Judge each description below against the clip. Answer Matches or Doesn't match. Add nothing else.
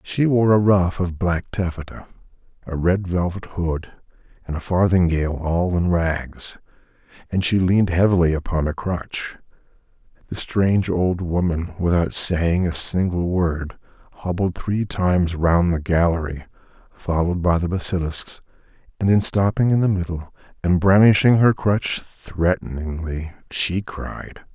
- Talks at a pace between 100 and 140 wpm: Matches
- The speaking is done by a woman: Doesn't match